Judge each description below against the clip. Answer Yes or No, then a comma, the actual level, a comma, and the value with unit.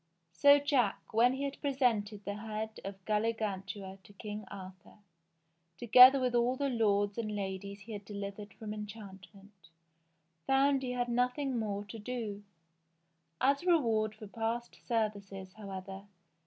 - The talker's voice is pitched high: Yes, high, 215 Hz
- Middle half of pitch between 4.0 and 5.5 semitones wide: No, average, 3.6 semitones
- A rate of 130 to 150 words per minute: Yes, average, 140 wpm